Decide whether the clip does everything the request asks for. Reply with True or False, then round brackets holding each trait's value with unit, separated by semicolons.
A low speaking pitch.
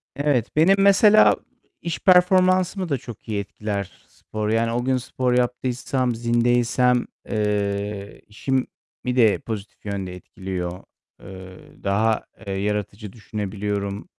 True (115 Hz)